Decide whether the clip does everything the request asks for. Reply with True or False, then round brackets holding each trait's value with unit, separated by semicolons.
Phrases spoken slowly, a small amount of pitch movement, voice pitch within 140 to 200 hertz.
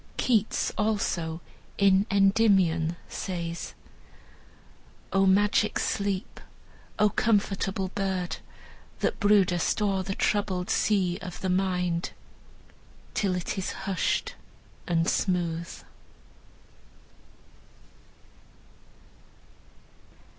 True (75 wpm; 2.1 semitones; 190 Hz)